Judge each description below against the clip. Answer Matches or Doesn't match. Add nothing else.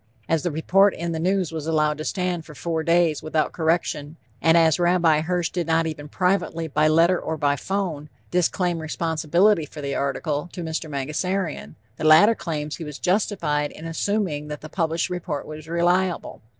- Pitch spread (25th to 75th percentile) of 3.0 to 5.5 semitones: Doesn't match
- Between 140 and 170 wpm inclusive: Doesn't match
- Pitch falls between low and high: Matches